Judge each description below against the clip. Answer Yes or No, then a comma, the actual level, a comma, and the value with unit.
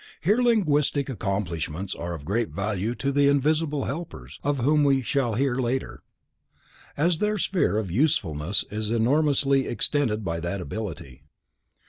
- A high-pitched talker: No, low, 125 Hz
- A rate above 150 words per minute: No, average, 140 wpm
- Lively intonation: Yes, wide, 6.7 semitones